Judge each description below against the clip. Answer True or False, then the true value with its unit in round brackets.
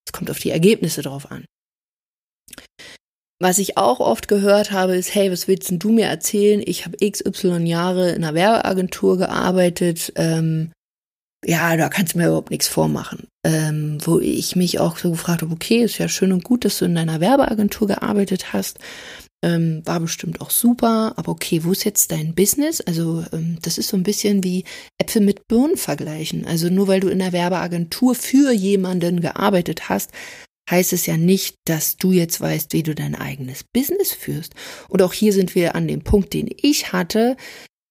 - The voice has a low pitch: False (185 Hz)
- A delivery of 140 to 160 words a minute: False (185 wpm)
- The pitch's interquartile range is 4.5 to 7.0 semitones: False (3.7 semitones)